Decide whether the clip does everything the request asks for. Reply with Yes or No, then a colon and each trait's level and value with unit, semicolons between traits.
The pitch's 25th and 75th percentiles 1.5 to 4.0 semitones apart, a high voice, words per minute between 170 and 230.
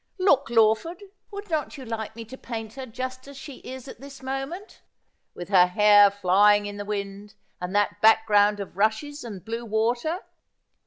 No: average, 4.7 semitones; high, 225 Hz; average, 175 wpm